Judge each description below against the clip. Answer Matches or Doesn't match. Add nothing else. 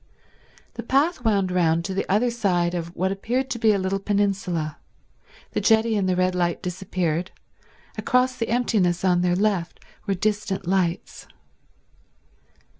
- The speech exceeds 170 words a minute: Doesn't match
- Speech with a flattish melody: Doesn't match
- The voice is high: Matches